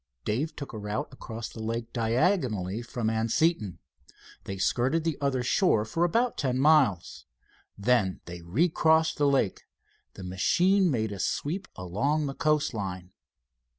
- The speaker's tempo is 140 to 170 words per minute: Yes, average, 145 wpm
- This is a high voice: No, low, 120 Hz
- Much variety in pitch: Yes, wide, 6.8 semitones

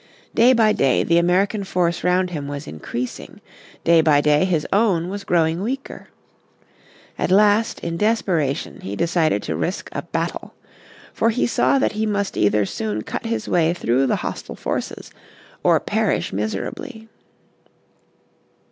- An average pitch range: No, wide, 6.5 semitones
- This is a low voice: No, medium, 175 Hz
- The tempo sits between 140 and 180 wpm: Yes, average, 145 wpm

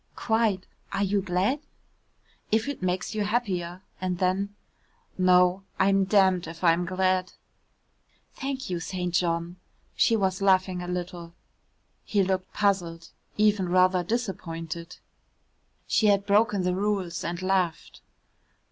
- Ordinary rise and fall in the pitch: No, narrow, 2.1 semitones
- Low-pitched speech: No, medium, 185 Hz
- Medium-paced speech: No, slow, 125 wpm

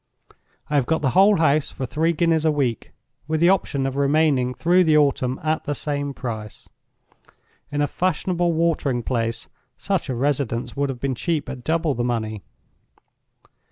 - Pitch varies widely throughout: No, average, 4.1 semitones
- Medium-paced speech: Yes, average, 170 wpm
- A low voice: No, medium, 145 Hz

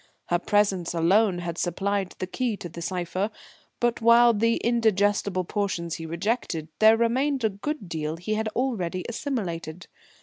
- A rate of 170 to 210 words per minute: No, average, 155 wpm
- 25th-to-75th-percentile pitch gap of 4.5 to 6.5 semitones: Yes, average, 4.8 semitones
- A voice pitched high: Yes, high, 200 Hz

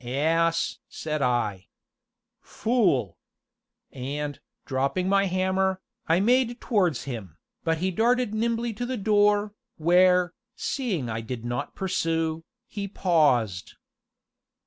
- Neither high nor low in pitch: Yes, medium, 175 Hz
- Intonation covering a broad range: Yes, wide, 7.0 semitones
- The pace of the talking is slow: Yes, slow, 110 wpm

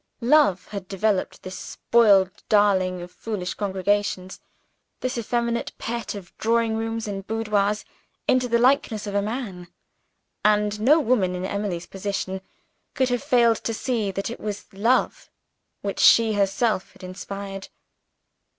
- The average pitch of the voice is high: Yes, high, 210 Hz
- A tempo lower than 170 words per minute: Yes, average, 140 wpm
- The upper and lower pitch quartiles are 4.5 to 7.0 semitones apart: No, average, 3.0 semitones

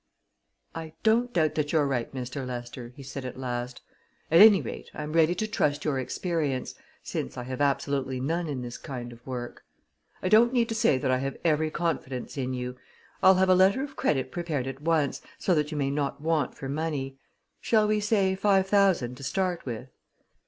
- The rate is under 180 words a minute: No, average, 200 wpm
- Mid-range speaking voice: Yes, medium, 145 Hz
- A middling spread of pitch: No, wide, 5.7 semitones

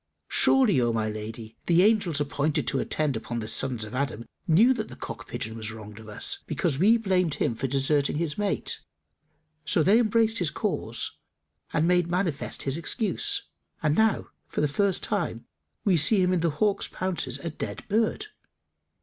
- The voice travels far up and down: Yes, wide, 7.4 semitones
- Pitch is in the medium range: Yes, medium, 155 Hz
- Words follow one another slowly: No, average, 180 wpm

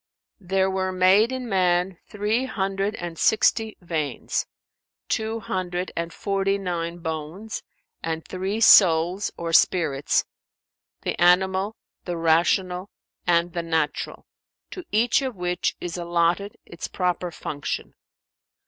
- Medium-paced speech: No, slow, 120 wpm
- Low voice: No, medium, 180 Hz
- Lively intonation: No, average, 2.8 semitones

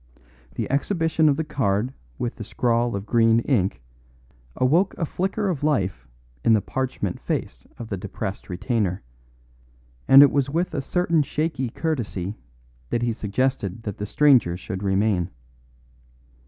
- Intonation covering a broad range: Yes, wide, 6.6 semitones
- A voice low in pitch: Yes, low, 120 Hz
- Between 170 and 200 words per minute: No, average, 145 wpm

